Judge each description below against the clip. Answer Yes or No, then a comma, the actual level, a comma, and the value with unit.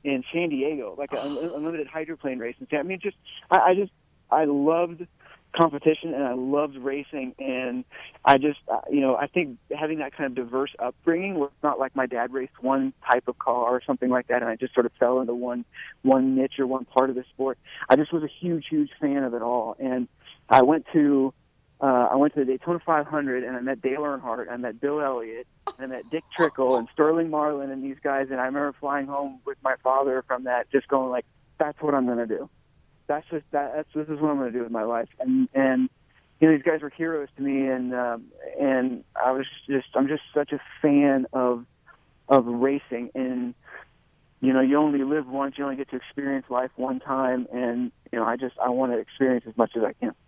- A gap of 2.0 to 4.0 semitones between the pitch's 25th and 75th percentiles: Yes, average, 2.7 semitones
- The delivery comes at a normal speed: No, fast, 225 wpm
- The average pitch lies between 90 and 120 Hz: No, low, 135 Hz